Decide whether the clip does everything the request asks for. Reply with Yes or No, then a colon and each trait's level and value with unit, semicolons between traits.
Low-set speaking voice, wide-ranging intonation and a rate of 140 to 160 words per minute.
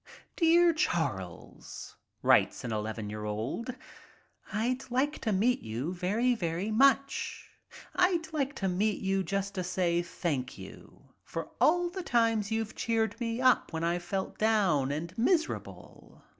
No: high, 210 Hz; wide, 6.9 semitones; average, 145 wpm